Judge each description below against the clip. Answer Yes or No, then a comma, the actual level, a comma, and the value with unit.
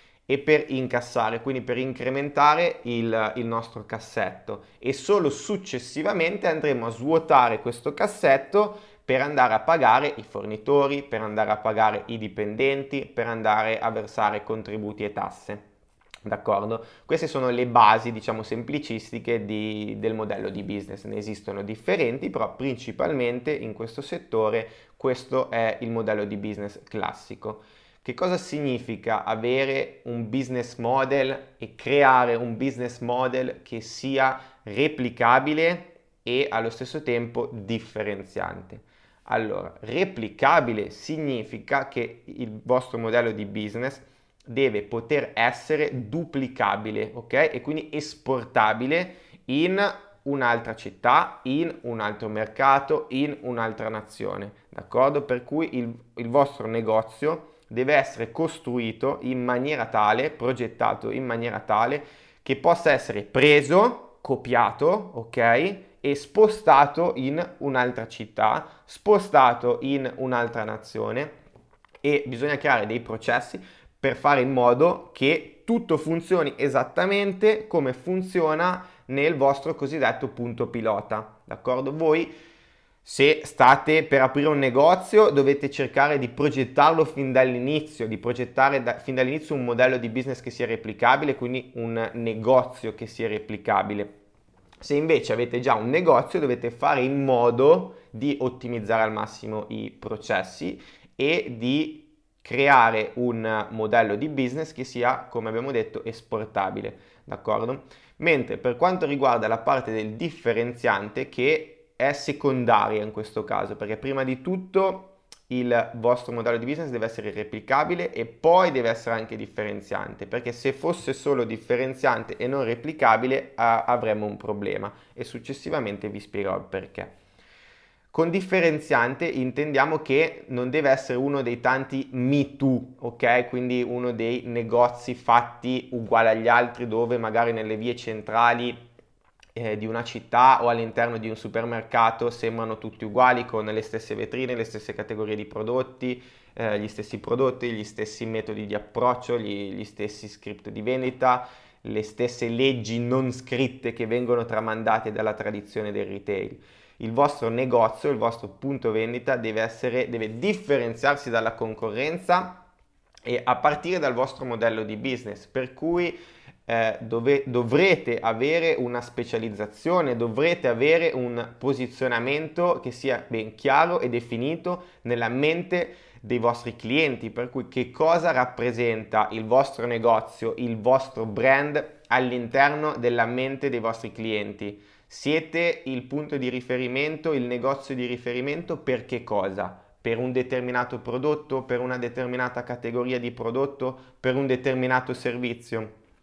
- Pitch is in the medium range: No, low, 125 Hz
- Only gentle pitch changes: No, average, 3.4 semitones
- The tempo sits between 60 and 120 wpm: No, average, 135 wpm